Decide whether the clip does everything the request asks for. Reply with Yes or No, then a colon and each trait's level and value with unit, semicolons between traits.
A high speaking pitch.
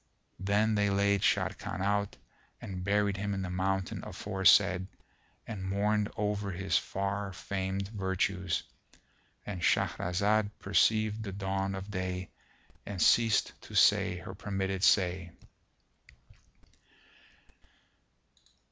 No: low, 100 Hz